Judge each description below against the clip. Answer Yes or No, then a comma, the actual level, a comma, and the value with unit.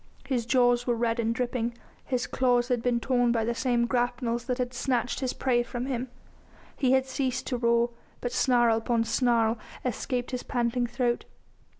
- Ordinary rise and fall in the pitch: No, narrow, 1.1 semitones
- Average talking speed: Yes, average, 180 wpm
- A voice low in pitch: No, high, 245 Hz